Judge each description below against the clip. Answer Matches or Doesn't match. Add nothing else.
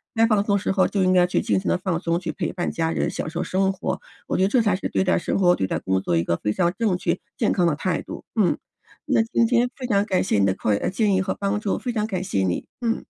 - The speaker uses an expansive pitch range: Doesn't match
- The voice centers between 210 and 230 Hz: Doesn't match